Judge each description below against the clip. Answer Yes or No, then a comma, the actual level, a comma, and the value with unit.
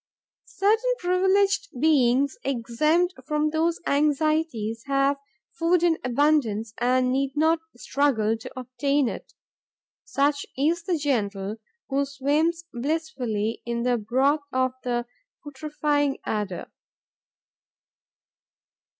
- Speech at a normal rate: No, slow, 100 wpm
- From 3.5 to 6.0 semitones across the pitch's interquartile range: Yes, average, 4.6 semitones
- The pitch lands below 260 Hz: No, very high, 280 Hz